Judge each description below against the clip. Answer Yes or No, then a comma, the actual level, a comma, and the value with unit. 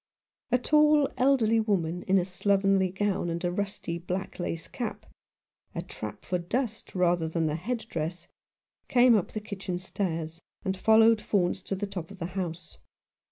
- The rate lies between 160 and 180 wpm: Yes, average, 175 wpm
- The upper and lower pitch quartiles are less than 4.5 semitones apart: Yes, average, 3.8 semitones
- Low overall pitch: No, high, 190 Hz